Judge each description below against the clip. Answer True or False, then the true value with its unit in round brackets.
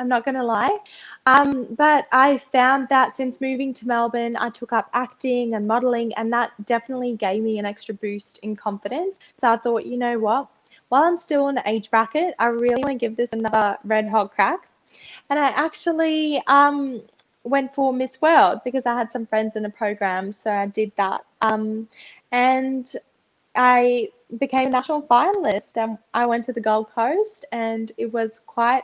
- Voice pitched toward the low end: False (245 Hz)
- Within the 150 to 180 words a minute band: False (190 wpm)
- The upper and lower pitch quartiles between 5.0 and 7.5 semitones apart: False (3.5 semitones)